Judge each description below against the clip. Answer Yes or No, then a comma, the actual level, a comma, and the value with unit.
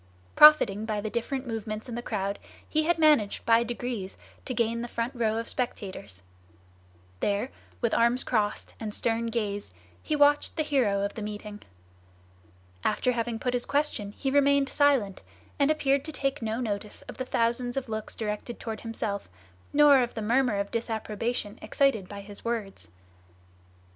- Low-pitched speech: No, high, 230 Hz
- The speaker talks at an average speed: Yes, average, 165 wpm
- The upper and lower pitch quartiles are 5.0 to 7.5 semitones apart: No, average, 3.8 semitones